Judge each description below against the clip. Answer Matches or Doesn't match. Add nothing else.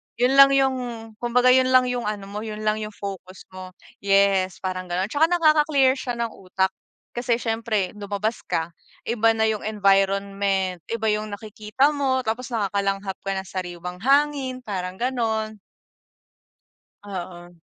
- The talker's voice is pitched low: Doesn't match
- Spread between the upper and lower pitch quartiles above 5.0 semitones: Doesn't match